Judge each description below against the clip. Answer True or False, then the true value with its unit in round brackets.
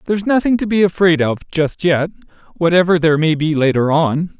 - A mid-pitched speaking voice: True (165 Hz)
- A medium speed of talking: True (190 wpm)